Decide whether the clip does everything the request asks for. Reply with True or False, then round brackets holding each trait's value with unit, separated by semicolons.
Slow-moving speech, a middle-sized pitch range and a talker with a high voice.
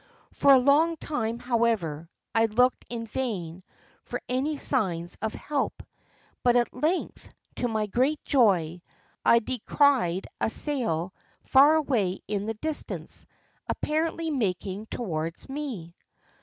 False (125 wpm; 6.6 semitones; 235 Hz)